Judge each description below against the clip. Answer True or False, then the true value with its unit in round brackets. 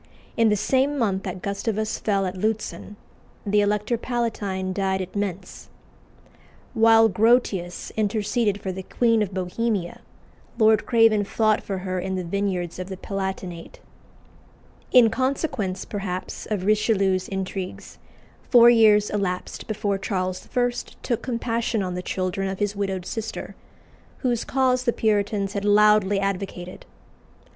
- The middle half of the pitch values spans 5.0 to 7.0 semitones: False (2.9 semitones)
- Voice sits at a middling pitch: False (205 Hz)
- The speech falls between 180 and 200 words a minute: False (135 wpm)